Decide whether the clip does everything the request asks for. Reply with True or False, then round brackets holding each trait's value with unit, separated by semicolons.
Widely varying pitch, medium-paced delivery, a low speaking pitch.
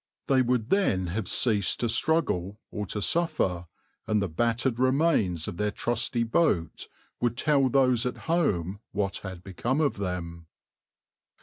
True (5.8 semitones; 145 wpm; 115 Hz)